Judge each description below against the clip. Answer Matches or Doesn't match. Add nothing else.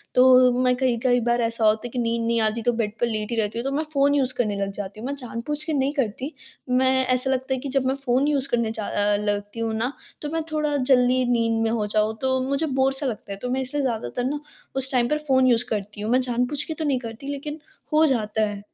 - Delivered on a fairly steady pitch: Doesn't match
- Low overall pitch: Doesn't match